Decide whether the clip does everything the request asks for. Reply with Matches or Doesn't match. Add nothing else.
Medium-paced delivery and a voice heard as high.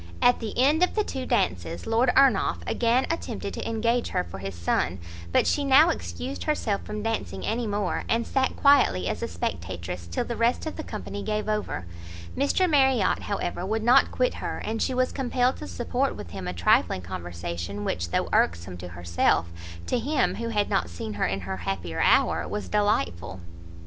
Matches